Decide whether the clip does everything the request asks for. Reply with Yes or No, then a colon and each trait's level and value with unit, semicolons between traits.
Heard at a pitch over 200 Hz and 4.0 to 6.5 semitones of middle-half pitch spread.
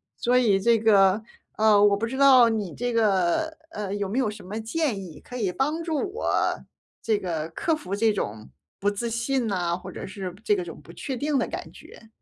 Yes: high, 215 Hz; average, 4.3 semitones